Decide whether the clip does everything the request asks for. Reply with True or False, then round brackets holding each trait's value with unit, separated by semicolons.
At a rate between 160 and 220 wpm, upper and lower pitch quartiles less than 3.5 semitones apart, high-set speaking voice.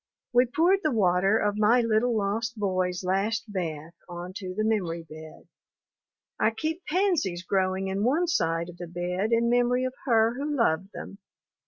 False (165 wpm; 5.0 semitones; 210 Hz)